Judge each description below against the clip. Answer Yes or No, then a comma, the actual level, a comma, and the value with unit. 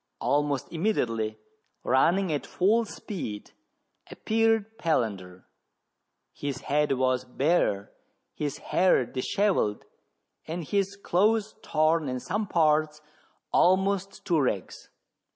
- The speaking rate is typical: No, slow, 100 wpm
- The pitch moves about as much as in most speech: No, wide, 7.2 semitones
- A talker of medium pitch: Yes, medium, 155 Hz